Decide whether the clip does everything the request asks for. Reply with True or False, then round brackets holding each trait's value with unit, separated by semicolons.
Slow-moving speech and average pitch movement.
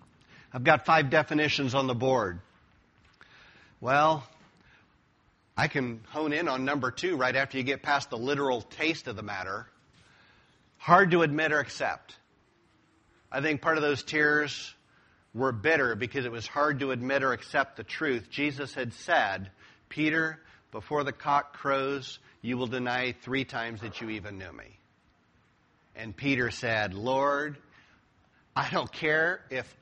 False (150 wpm; 4.1 semitones)